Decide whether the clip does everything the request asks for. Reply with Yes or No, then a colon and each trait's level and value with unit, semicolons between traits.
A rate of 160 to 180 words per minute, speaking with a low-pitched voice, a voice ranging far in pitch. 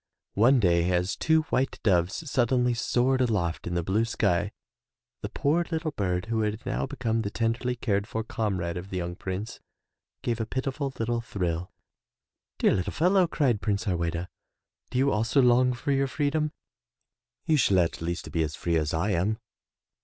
Yes: average, 175 wpm; low, 110 Hz; wide, 6.2 semitones